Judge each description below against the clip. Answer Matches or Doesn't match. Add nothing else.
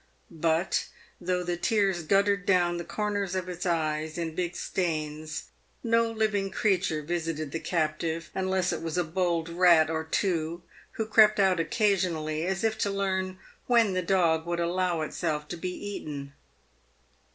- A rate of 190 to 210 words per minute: Doesn't match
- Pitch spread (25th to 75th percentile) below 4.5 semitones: Matches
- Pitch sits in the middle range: Matches